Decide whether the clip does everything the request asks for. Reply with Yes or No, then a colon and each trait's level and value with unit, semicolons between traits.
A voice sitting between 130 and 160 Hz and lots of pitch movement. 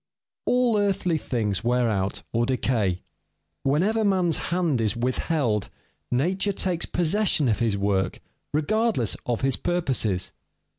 Yes: low, 135 Hz; wide, 8.2 semitones